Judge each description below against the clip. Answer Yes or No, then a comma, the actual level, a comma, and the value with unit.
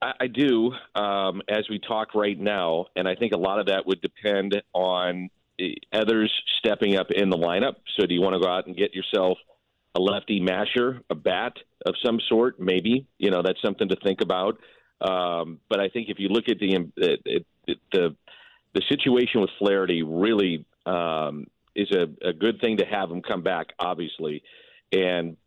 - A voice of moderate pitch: No, low, 100 Hz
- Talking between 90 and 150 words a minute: No, average, 190 wpm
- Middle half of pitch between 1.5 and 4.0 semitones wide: Yes, average, 3.3 semitones